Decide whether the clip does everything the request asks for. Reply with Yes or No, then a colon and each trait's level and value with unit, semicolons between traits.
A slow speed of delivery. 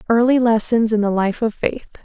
No: fast, 205 wpm